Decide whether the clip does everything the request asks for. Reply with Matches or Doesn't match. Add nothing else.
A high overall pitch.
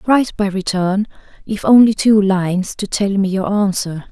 Matches